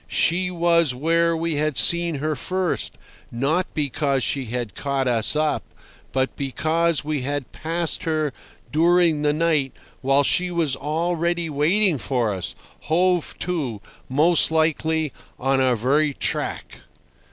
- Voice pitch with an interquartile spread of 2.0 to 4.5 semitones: Yes, average, 3.6 semitones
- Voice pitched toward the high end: No, medium, 155 Hz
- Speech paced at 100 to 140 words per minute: Yes, slow, 135 wpm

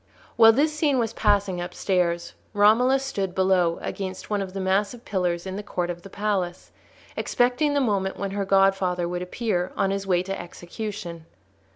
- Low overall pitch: No, high, 195 Hz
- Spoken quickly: No, average, 175 wpm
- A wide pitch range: No, average, 3.1 semitones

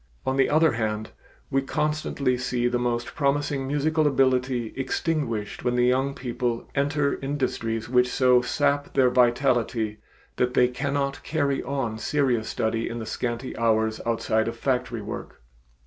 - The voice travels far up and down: No, average, 2.9 semitones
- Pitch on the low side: Yes, low, 125 Hz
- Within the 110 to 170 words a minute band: Yes, average, 150 wpm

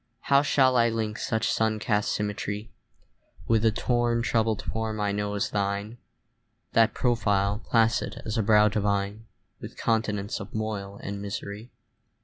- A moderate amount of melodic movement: No, narrow, 1.7 semitones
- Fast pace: No, average, 145 wpm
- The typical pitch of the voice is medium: No, low, 110 Hz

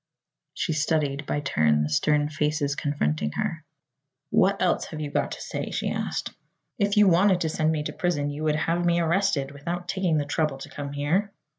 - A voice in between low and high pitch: Yes, medium, 150 Hz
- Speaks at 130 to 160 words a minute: No, average, 195 wpm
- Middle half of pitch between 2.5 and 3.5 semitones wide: Yes, average, 3.1 semitones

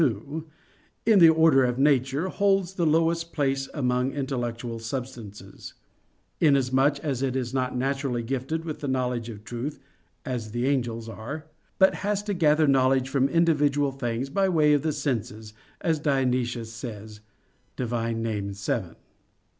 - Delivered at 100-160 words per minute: Yes, average, 145 wpm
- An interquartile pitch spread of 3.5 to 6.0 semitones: Yes, average, 4.1 semitones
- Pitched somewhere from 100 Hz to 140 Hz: Yes, low, 135 Hz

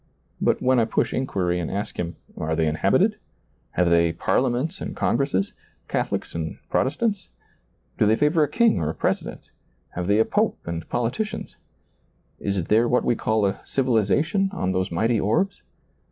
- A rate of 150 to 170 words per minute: Yes, average, 165 wpm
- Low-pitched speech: Yes, low, 110 Hz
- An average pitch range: No, wide, 7.2 semitones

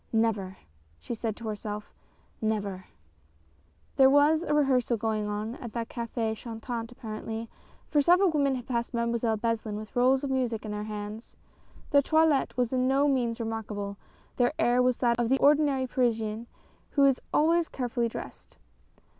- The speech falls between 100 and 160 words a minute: No, average, 170 wpm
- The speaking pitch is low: No, high, 235 Hz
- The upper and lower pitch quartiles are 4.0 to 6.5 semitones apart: No, average, 3.5 semitones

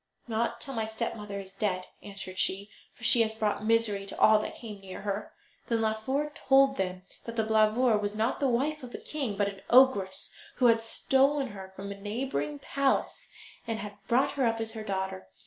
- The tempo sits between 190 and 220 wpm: Yes, average, 200 wpm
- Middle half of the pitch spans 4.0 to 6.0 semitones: No, average, 3.3 semitones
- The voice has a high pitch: Yes, high, 220 Hz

